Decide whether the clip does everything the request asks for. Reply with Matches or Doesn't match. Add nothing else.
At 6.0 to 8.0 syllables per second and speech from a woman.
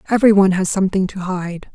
Matches